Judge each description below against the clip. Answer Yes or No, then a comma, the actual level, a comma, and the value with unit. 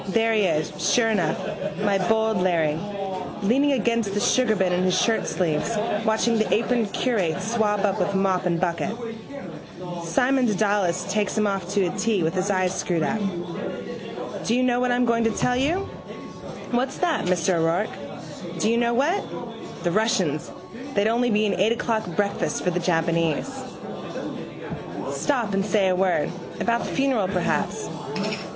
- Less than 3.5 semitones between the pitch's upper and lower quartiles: No, average, 4.1 semitones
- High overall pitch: Yes, high, 205 Hz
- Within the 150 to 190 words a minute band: Yes, average, 160 wpm